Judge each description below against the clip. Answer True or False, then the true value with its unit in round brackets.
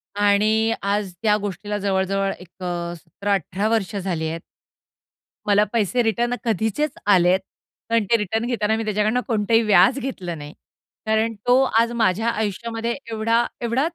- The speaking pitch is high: True (210 Hz)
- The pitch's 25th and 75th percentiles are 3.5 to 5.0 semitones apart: False (2.8 semitones)